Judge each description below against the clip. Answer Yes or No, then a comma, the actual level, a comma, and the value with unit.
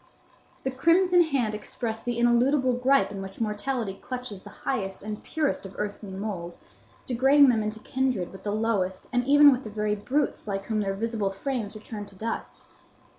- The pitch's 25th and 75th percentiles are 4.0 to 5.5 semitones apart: Yes, average, 4.3 semitones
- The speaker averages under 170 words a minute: No, average, 180 wpm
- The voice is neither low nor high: No, high, 225 Hz